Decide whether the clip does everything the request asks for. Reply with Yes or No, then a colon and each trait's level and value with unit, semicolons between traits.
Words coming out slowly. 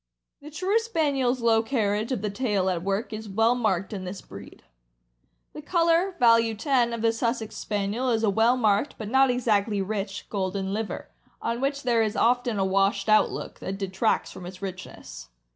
No: average, 185 wpm